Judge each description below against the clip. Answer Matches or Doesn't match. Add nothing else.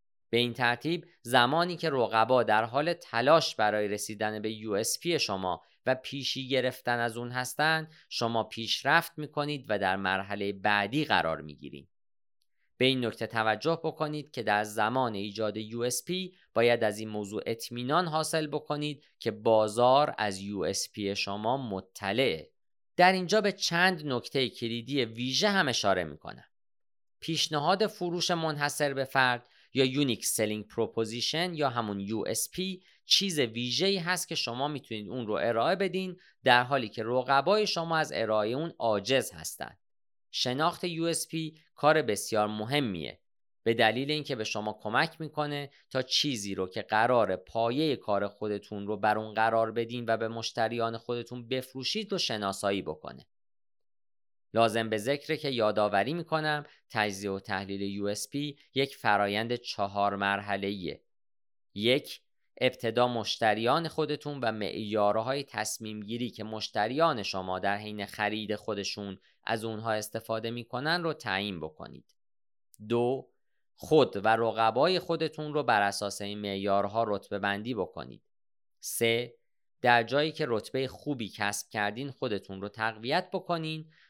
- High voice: Doesn't match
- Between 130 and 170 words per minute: Matches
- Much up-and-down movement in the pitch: Matches